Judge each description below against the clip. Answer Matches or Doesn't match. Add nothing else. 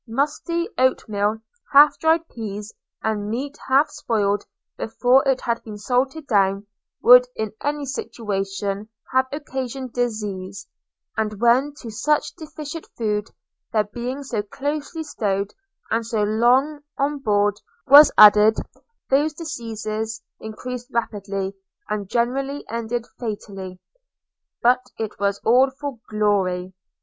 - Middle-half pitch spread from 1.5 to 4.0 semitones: Doesn't match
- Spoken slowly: Matches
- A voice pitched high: Matches